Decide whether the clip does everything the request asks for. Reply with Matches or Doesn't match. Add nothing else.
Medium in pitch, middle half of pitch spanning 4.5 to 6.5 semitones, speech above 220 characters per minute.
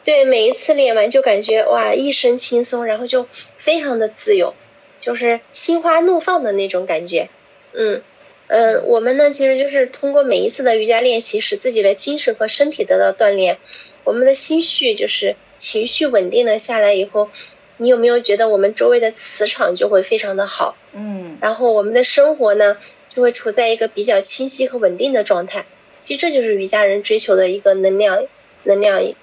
Doesn't match